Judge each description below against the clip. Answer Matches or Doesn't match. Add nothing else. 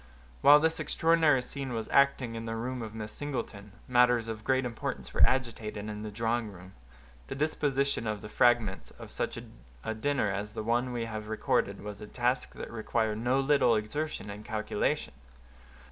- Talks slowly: Doesn't match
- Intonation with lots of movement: Doesn't match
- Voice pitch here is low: Matches